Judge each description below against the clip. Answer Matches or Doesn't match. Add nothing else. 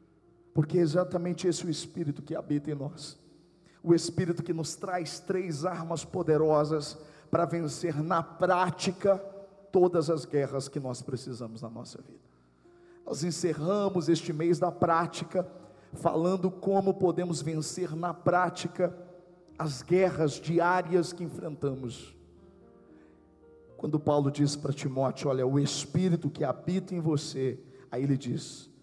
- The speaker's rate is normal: Matches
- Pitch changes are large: Doesn't match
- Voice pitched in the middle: Matches